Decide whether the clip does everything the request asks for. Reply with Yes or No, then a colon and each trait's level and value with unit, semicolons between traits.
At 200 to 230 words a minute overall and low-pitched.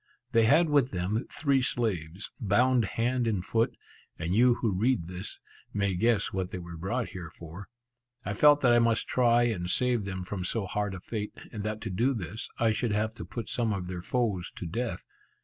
Yes: fast, 205 wpm; low, 110 Hz